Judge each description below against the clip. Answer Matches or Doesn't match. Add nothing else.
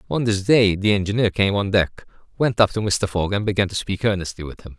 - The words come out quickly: Matches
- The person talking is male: Matches